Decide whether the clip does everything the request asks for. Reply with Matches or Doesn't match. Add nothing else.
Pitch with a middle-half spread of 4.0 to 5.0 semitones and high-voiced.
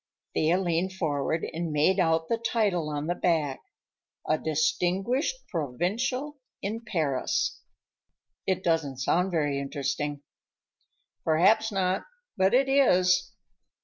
Doesn't match